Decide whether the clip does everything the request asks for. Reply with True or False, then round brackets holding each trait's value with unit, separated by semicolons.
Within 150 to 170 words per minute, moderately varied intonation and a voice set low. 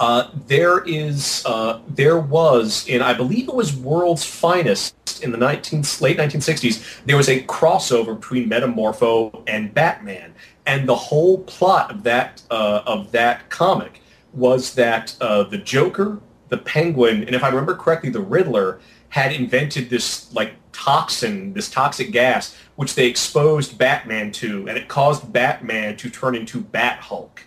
True (155 wpm; 4.6 semitones; 130 Hz)